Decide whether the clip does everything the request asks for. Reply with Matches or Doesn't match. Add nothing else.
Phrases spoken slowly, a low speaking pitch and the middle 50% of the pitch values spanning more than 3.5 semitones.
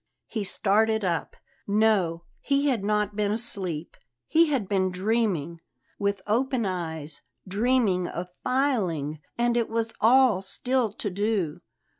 Doesn't match